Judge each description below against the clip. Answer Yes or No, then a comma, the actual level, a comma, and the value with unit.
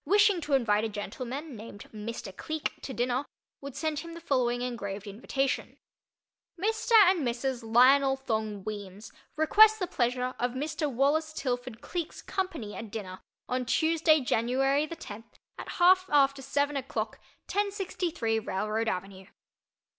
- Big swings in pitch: Yes, wide, 5.7 semitones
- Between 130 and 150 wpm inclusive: Yes, average, 140 wpm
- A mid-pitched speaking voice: No, very high, 260 Hz